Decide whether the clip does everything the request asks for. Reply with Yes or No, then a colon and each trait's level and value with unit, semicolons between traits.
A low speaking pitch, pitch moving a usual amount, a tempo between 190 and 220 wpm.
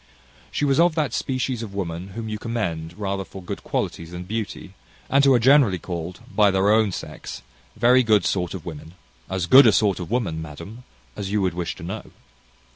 Yes: low, 100 Hz; average, 4.8 semitones; average, 200 wpm